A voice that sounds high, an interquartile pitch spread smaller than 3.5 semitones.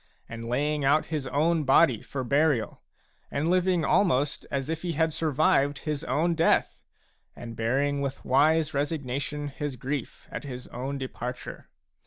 No: medium, 145 Hz; average, 2.9 semitones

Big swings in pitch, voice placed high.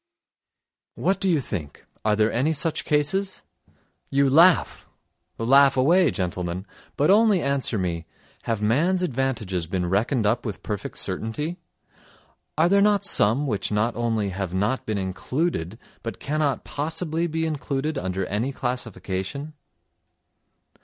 No: wide, 7.2 semitones; low, 130 Hz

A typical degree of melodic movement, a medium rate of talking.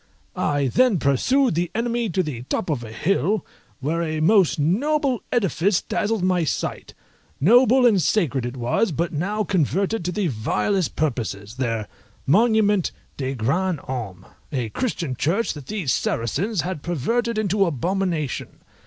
No: wide, 7.4 semitones; average, 145 wpm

